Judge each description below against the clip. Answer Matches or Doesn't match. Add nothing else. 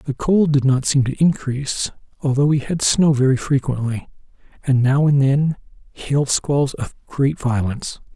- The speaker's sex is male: Matches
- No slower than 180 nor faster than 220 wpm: Doesn't match